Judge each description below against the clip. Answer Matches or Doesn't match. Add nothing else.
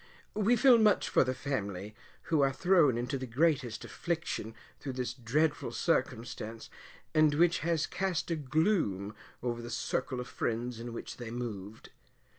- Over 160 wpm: Doesn't match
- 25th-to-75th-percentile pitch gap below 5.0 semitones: Doesn't match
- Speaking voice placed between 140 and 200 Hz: Doesn't match